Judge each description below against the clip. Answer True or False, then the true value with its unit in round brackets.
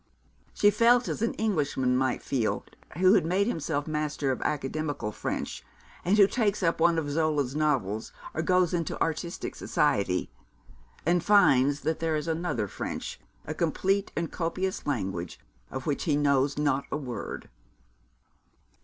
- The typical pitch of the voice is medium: True (155 Hz)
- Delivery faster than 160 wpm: False (150 wpm)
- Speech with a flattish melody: False (4.4 semitones)